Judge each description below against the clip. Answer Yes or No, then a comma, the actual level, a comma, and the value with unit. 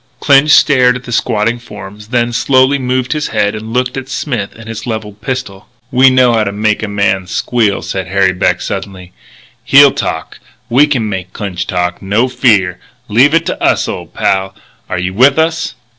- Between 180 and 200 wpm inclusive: Yes, average, 190 wpm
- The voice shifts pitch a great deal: No, average, 4.6 semitones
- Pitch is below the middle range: Yes, low, 110 Hz